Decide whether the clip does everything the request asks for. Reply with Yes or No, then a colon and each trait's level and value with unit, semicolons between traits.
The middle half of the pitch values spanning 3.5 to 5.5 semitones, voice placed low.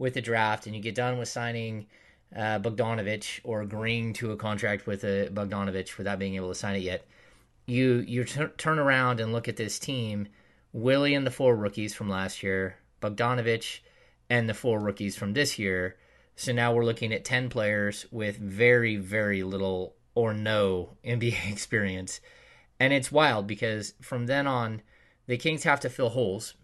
No: average, 3.1 semitones; low, 110 Hz